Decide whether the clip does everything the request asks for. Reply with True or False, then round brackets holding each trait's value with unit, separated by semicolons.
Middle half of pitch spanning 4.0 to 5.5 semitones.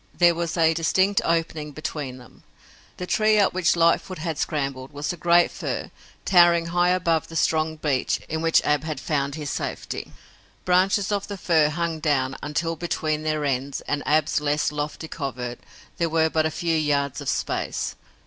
False (2.6 semitones)